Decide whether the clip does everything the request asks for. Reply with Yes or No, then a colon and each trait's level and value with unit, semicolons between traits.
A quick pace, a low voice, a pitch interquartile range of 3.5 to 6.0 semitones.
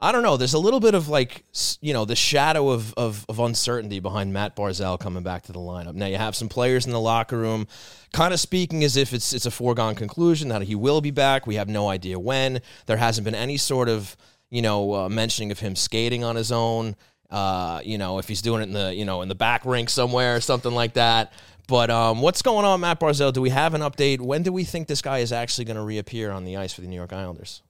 Yes: fast, 260 wpm; low, 115 Hz; average, 4.4 semitones